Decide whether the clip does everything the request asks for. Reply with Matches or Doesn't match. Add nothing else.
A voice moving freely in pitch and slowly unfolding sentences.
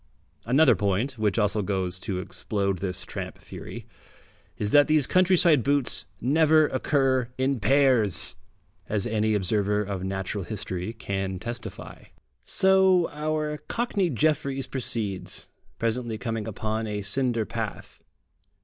Matches